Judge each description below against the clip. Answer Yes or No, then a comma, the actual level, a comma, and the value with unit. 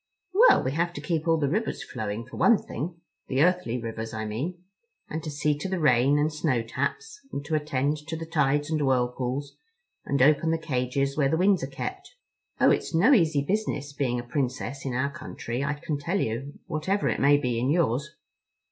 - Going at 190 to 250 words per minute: Yes, average, 200 wpm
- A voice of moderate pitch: Yes, medium, 145 Hz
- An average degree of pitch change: Yes, average, 4.2 semitones